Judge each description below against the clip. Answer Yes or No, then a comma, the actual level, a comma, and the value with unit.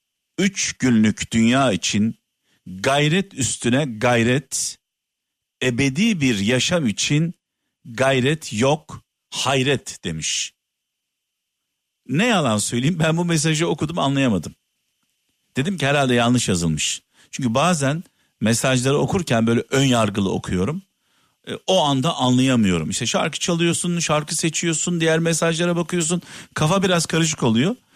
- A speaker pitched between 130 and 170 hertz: Yes, medium, 140 Hz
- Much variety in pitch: Yes, wide, 5.8 semitones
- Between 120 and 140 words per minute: No, average, 110 wpm